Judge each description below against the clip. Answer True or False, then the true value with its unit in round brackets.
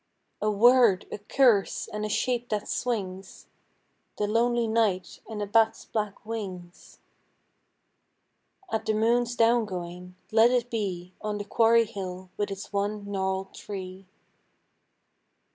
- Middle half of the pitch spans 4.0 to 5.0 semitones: False (3.0 semitones)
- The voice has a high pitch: True (210 Hz)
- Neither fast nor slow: False (130 wpm)